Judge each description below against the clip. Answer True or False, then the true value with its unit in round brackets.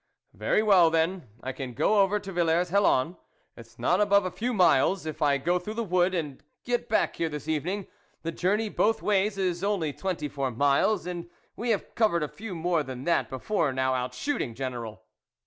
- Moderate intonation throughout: False (5.8 semitones)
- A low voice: False (175 Hz)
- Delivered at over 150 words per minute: True (200 wpm)